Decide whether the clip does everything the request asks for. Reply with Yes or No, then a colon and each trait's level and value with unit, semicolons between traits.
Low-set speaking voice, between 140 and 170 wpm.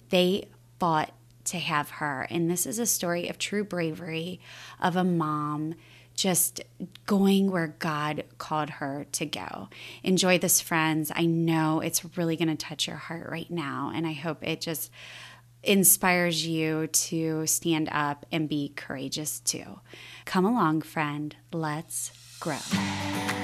No: medium, 160 Hz; average, 145 wpm